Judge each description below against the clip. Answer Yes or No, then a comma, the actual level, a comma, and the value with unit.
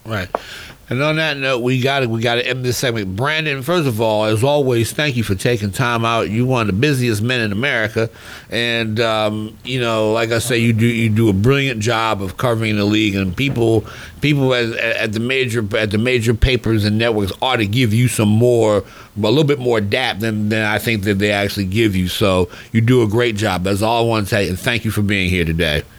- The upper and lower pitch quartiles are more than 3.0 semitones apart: No, narrow, 2.5 semitones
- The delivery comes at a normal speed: No, fast, 240 wpm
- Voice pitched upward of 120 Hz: No, low, 115 Hz